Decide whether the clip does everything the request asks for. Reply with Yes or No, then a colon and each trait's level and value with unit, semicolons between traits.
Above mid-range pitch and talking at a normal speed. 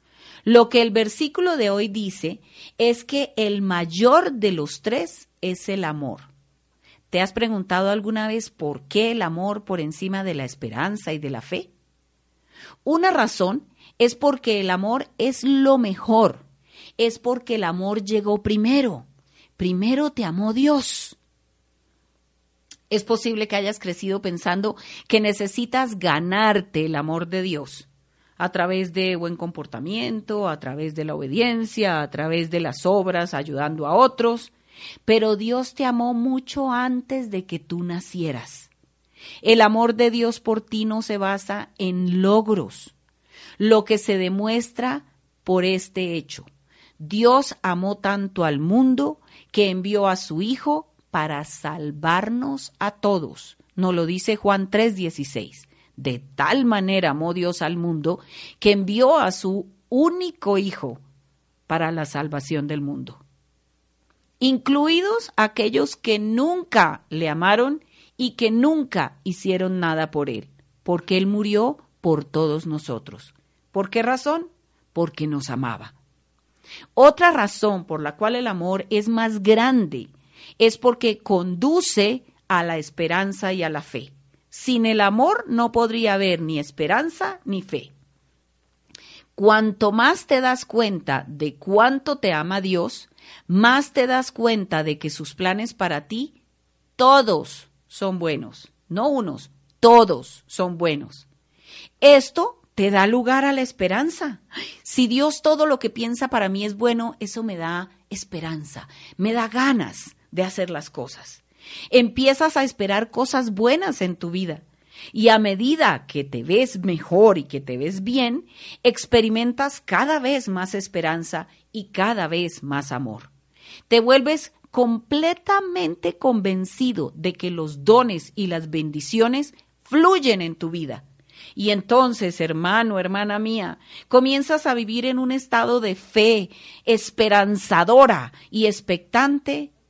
Yes: high, 200 Hz; average, 140 wpm